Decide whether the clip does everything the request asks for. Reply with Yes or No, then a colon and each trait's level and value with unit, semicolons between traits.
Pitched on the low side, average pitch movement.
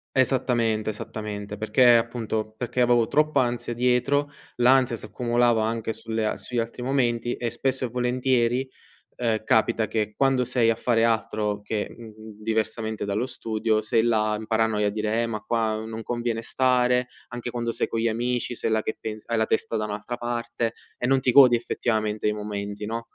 No: low, 115 Hz; narrow, 2.1 semitones